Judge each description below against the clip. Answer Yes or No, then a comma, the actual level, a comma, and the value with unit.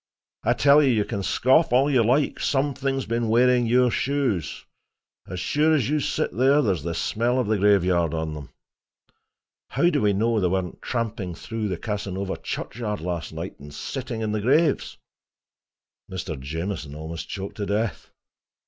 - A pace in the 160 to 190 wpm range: Yes, average, 170 wpm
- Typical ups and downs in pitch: No, wide, 5.9 semitones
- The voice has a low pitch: Yes, low, 110 Hz